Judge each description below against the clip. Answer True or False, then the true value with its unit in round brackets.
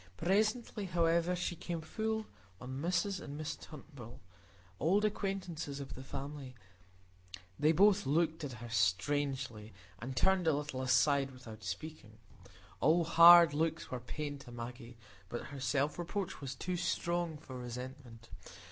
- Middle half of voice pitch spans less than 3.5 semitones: False (5.1 semitones)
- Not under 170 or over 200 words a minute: False (140 wpm)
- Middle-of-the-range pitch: True (150 Hz)